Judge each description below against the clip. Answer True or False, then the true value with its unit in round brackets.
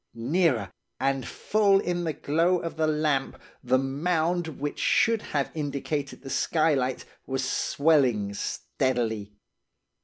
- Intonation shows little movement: False (4.0 semitones)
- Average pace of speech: False (120 wpm)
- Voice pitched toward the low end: False (145 Hz)